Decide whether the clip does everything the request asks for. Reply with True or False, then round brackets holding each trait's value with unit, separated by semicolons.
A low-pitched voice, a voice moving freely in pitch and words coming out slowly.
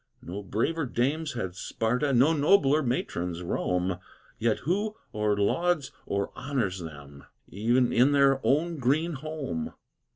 True (125 Hz; 7.1 semitones; 130 wpm)